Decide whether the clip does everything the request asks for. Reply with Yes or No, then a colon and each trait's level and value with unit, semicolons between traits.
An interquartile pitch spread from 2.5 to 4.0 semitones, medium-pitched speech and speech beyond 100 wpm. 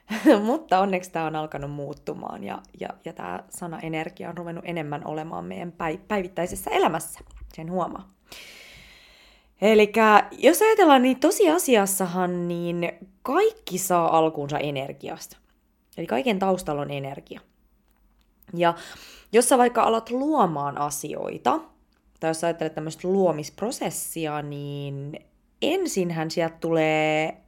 No: average, 5.1 semitones; medium, 175 Hz; average, 115 wpm